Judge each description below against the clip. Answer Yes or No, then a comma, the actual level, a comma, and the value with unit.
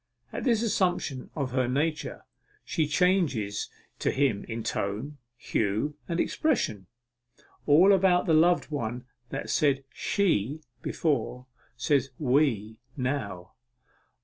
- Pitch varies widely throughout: Yes, wide, 5.9 semitones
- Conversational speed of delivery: No, slow, 115 wpm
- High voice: No, medium, 140 Hz